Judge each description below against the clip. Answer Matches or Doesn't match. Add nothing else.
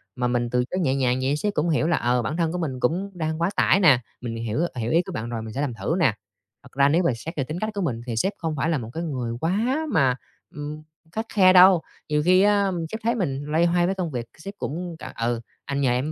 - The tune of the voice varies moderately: Doesn't match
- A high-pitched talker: Doesn't match